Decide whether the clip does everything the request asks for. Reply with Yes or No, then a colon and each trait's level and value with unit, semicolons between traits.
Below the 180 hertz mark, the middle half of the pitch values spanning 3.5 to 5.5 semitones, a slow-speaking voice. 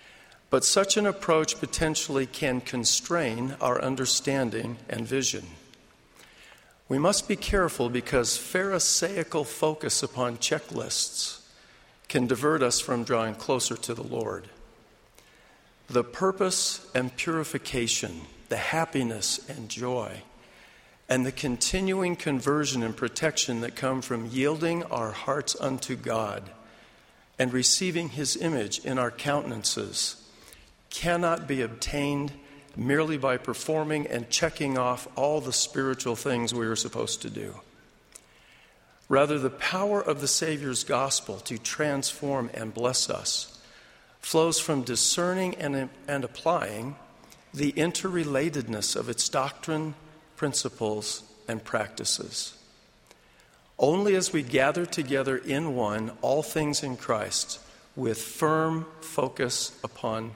Yes: low, 135 Hz; average, 4.5 semitones; slow, 115 wpm